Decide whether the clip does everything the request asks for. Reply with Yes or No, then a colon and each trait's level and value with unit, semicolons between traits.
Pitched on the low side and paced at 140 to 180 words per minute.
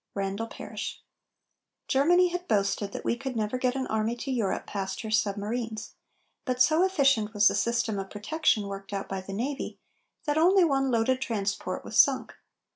No: high, 230 Hz; average, 175 wpm